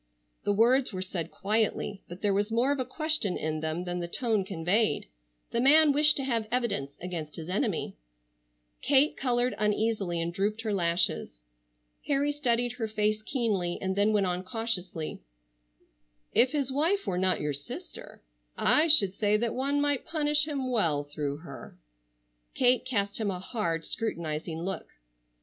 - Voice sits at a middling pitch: No, high, 210 Hz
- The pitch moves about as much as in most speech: No, wide, 6.3 semitones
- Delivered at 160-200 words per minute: Yes, average, 165 wpm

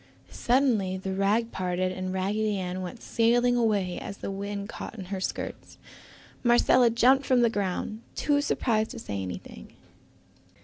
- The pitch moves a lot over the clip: No, average, 4.1 semitones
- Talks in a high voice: Yes, high, 205 Hz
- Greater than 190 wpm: No, average, 150 wpm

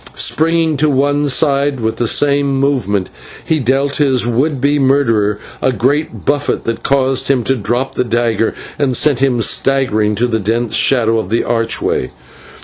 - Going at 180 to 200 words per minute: No, average, 165 wpm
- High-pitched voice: No, low, 130 Hz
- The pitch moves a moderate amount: Yes, average, 3.6 semitones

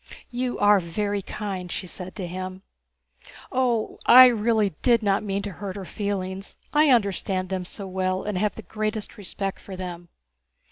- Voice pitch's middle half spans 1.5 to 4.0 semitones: Yes, narrow, 2.4 semitones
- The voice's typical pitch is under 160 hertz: No, high, 200 Hz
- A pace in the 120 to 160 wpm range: No, average, 170 wpm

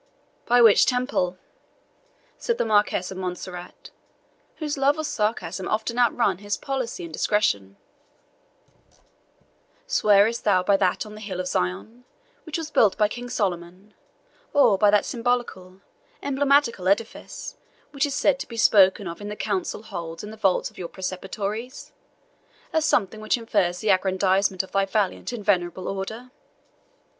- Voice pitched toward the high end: Yes, high, 210 Hz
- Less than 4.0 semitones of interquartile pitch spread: No, average, 4.3 semitones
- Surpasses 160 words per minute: No, average, 150 wpm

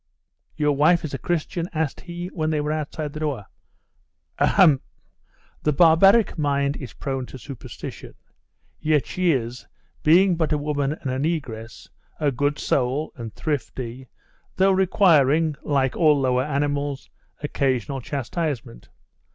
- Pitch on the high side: No, medium, 145 Hz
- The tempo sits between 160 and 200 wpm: No, slow, 135 wpm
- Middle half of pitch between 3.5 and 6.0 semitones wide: No, average, 3.0 semitones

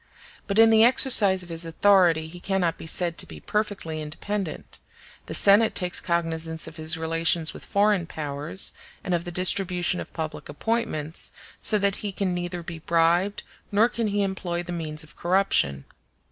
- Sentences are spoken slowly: No, average, 175 wpm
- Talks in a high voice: No, medium, 175 Hz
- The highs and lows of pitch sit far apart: No, average, 3.5 semitones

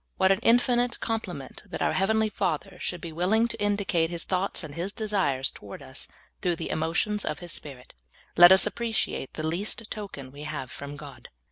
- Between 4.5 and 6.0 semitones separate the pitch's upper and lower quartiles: Yes, average, 5.2 semitones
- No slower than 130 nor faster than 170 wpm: No, average, 200 wpm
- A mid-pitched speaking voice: Yes, medium, 180 Hz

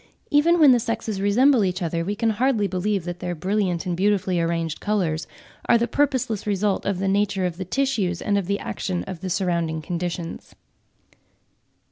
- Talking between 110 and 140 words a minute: No, average, 180 wpm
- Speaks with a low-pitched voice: No, high, 195 Hz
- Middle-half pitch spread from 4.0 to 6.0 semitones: No, average, 3.4 semitones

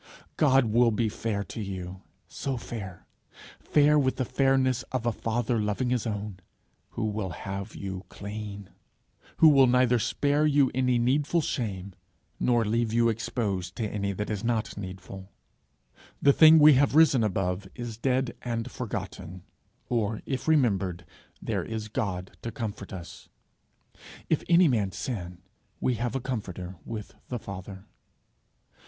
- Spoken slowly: No, average, 150 wpm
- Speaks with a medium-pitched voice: No, low, 115 Hz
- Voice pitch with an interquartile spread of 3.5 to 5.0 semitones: Yes, average, 4.4 semitones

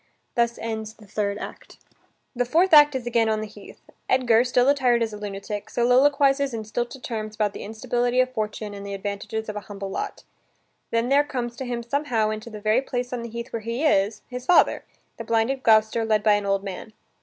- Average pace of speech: No, fast, 210 wpm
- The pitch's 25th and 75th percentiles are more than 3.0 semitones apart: No, average, 2.7 semitones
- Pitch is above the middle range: Yes, high, 230 Hz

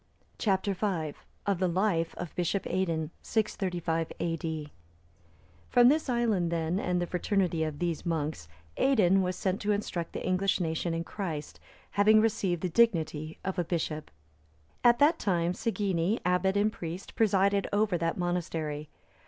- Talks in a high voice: No, medium, 180 Hz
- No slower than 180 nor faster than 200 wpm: No, average, 150 wpm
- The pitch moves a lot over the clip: No, average, 3.5 semitones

